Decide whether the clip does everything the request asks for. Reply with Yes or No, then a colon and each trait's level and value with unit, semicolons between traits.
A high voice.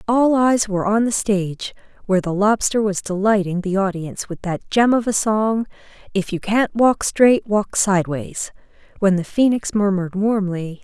Yes: high, 205 Hz